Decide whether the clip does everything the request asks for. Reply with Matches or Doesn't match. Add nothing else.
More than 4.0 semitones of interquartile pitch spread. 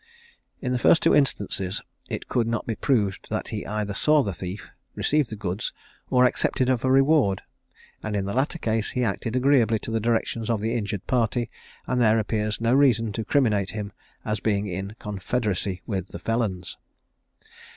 Doesn't match